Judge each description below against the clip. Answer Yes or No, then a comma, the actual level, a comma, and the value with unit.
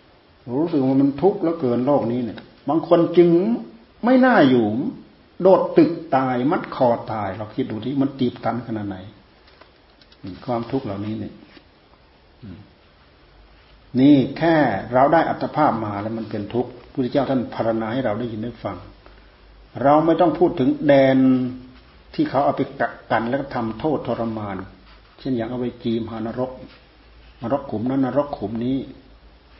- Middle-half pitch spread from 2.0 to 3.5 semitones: No, average, 4.4 semitones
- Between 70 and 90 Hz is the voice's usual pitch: No, low, 125 Hz